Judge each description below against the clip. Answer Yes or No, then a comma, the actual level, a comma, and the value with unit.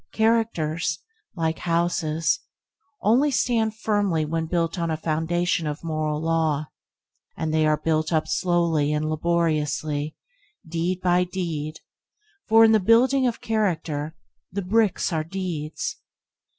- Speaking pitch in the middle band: Yes, medium, 165 Hz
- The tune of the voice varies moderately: Yes, average, 3.6 semitones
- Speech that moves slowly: Yes, slow, 125 wpm